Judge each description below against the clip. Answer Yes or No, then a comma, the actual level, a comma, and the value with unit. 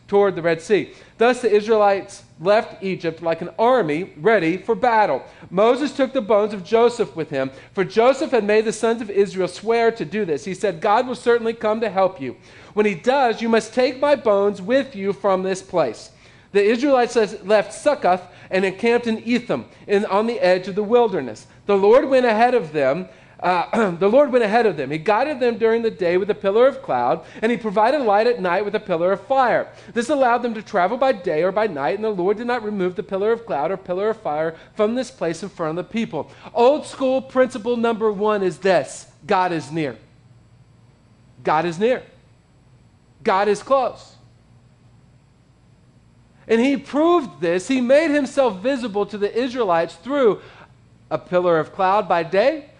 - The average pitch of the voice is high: Yes, high, 210 Hz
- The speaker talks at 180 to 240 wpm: Yes, average, 195 wpm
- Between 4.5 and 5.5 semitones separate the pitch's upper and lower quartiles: Yes, average, 4.9 semitones